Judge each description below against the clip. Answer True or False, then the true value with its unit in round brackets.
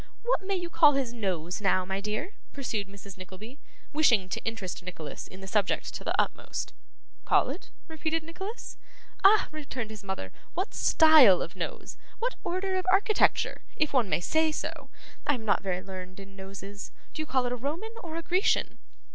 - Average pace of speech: True (185 wpm)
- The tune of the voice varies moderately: False (9.0 semitones)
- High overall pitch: True (245 Hz)